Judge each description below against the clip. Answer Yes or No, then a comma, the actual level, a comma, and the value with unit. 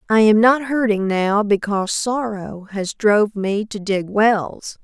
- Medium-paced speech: Yes, average, 160 wpm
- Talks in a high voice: Yes, high, 210 Hz